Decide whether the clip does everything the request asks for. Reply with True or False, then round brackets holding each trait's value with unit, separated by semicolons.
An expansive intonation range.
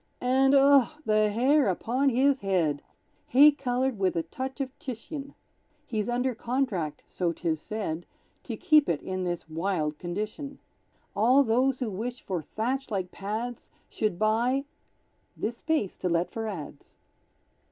True (6.2 semitones)